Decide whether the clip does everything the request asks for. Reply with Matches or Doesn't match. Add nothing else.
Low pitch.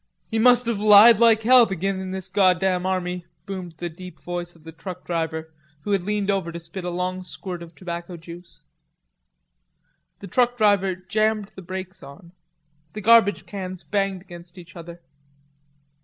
Doesn't match